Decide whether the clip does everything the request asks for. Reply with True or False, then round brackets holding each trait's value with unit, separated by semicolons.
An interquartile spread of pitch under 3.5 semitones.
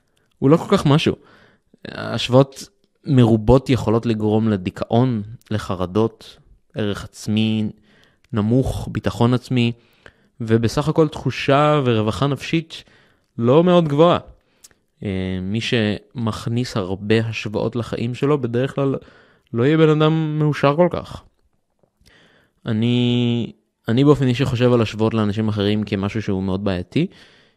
False (4.1 semitones)